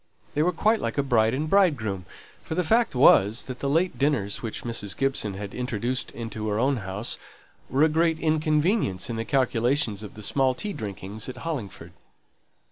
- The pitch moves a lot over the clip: Yes, wide, 6.2 semitones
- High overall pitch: No, low, 125 Hz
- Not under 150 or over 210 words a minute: Yes, average, 180 wpm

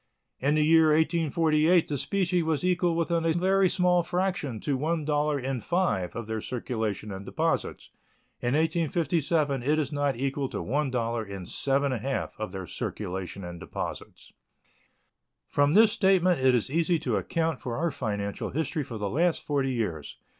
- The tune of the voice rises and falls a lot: Yes, wide, 5.7 semitones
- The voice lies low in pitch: No, medium, 145 Hz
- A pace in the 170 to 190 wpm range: Yes, average, 175 wpm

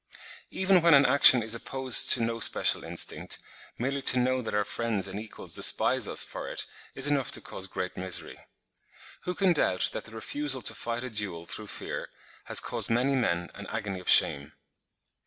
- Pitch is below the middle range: Yes, low, 115 Hz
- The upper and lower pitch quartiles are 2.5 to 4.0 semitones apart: No, average, 4.9 semitones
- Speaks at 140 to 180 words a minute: No, average, 190 wpm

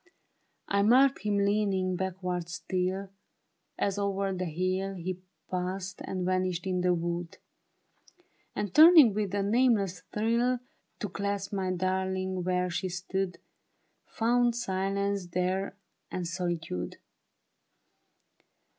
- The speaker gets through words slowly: Yes, slow, 110 wpm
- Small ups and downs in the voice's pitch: Yes, narrow, 1.7 semitones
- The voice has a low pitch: No, high, 190 Hz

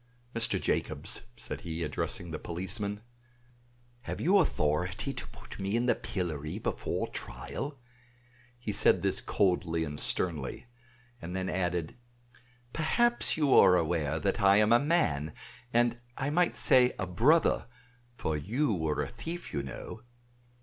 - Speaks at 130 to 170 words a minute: Yes, average, 145 wpm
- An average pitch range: No, wide, 6.9 semitones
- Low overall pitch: Yes, very low, 95 Hz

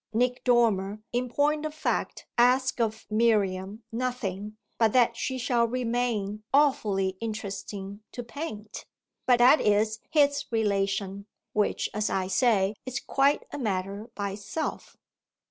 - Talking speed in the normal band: No, slow, 130 wpm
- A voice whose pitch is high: Yes, high, 225 Hz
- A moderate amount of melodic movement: Yes, average, 3.7 semitones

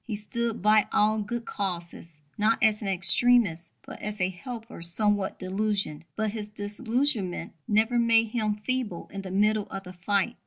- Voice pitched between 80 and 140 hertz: No, high, 210 Hz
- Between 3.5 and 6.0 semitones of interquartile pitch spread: No, average, 2.8 semitones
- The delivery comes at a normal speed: Yes, average, 165 wpm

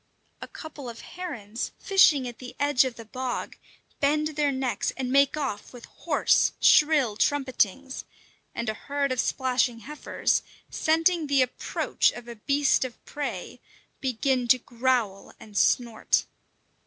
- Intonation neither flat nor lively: Yes, average, 3.2 semitones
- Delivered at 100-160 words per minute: Yes, average, 140 wpm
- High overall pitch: Yes, very high, 260 Hz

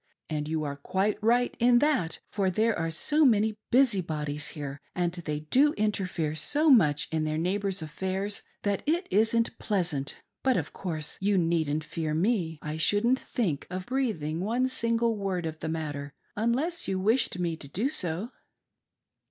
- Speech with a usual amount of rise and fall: No, wide, 6.5 semitones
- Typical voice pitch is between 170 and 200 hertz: Yes, high, 190 Hz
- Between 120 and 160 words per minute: No, average, 170 wpm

